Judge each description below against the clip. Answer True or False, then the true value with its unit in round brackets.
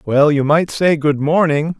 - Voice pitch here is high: False (155 Hz)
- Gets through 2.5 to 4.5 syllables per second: True (4.2 syllables/s)